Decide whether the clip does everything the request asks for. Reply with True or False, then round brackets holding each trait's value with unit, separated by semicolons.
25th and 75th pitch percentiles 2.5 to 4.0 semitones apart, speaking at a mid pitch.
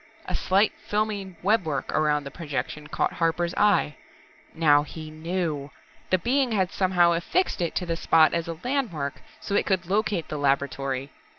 False (4.4 semitones; 170 Hz)